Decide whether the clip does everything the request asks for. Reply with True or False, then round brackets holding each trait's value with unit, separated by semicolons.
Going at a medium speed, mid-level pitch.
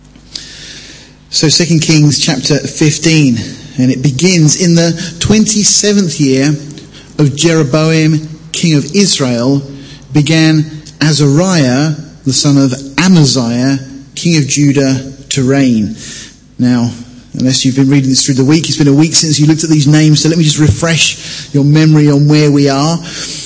True (150 wpm; 150 Hz)